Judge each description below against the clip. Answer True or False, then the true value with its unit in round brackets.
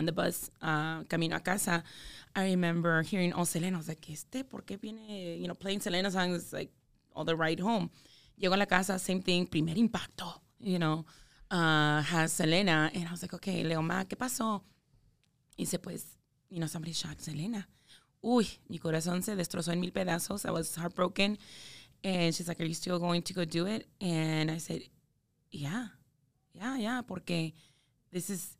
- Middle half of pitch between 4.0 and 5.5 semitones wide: False (2.8 semitones)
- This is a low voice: False (175 Hz)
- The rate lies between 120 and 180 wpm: False (190 wpm)